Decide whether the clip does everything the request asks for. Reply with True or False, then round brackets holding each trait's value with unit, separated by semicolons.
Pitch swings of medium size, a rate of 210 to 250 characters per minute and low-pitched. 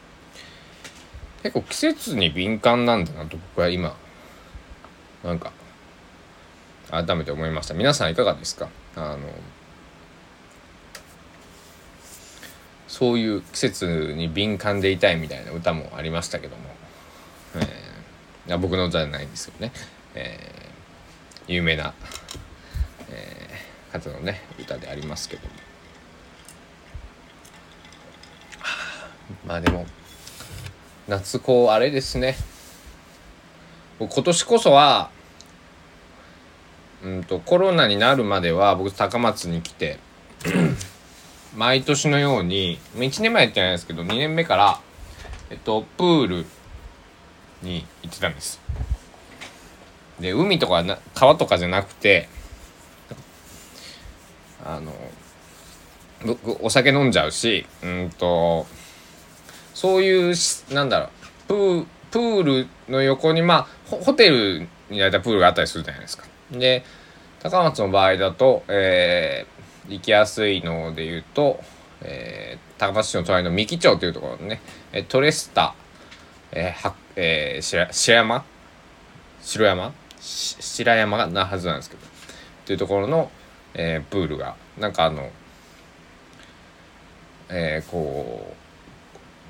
True (3.4 semitones; 220 characters per minute; 85 Hz)